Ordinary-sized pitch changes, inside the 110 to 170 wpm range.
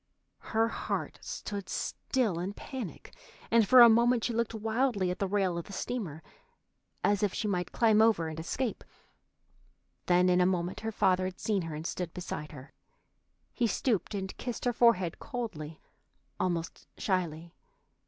Yes: average, 4.3 semitones; average, 165 wpm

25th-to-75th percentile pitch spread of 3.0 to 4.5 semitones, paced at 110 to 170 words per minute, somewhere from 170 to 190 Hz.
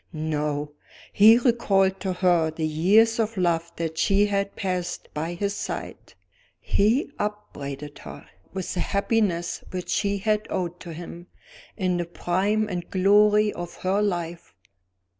Yes: average, 3.4 semitones; average, 140 wpm; medium, 185 Hz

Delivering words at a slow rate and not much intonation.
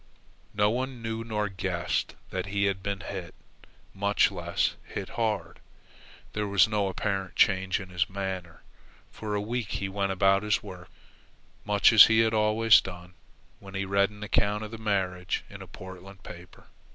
No: average, 170 wpm; narrow, 2.0 semitones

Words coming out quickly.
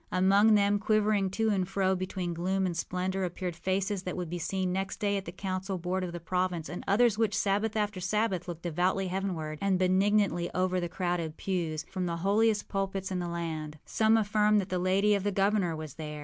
Yes: fast, 210 wpm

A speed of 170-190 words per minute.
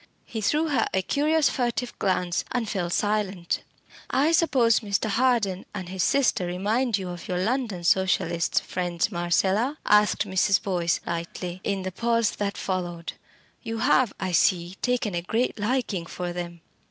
No: average, 155 wpm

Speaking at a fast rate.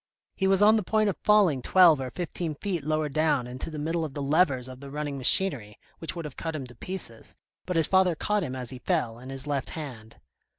Yes: fast, 240 wpm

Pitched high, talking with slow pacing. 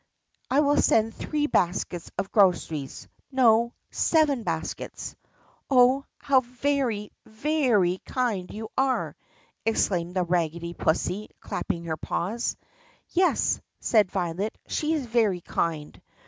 Yes: high, 220 Hz; slow, 120 wpm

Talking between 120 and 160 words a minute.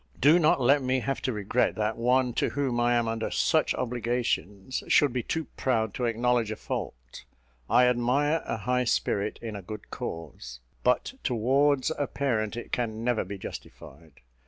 No: average, 175 wpm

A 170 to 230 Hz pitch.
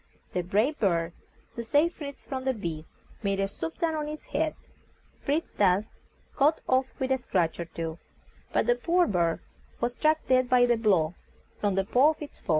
No: high, 240 Hz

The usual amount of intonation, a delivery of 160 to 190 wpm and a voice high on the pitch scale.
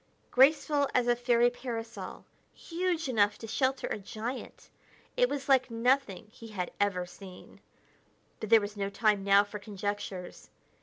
No: average, 4.3 semitones; average, 150 wpm; high, 225 Hz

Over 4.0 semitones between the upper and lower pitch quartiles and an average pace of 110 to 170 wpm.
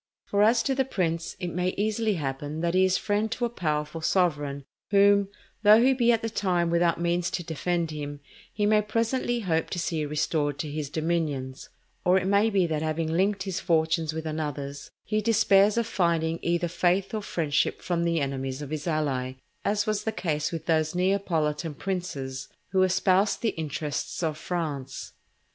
No: average, 4.7 semitones; average, 185 wpm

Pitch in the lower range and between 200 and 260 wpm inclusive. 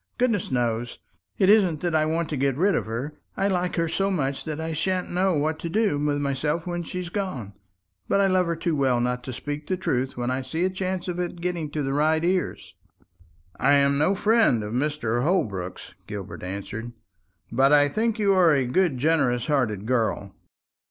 No: medium, 155 Hz; fast, 205 wpm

